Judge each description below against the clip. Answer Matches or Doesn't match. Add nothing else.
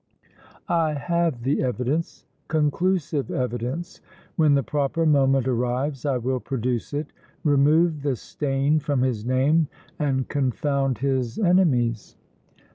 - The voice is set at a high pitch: Doesn't match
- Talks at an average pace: Doesn't match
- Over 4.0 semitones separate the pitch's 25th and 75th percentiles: Doesn't match